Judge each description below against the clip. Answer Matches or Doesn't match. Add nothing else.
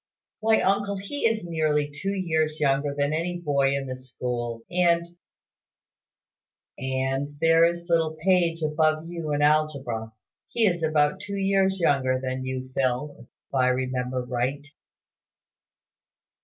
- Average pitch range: Matches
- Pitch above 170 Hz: Doesn't match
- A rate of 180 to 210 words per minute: Doesn't match